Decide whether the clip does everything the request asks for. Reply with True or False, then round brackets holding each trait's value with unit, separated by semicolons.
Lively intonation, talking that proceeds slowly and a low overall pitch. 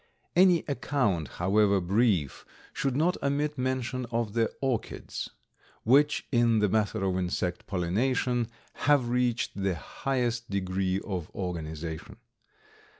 True (5.7 semitones; 115 wpm; 115 Hz)